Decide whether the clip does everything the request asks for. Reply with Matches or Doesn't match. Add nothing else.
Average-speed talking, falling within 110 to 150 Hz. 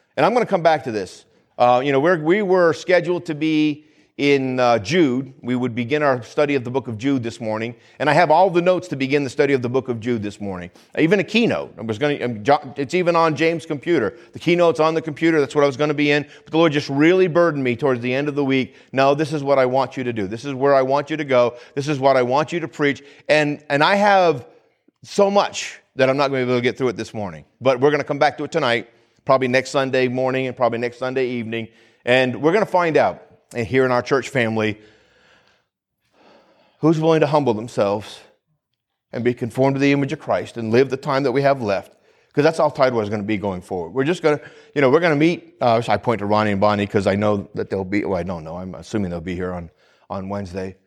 Doesn't match